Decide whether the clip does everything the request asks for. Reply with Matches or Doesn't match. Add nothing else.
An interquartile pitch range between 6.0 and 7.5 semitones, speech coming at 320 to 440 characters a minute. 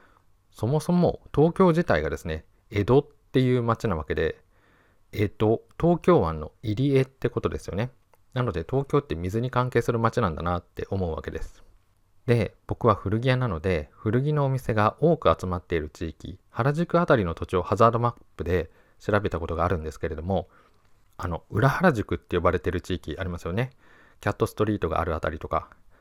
Doesn't match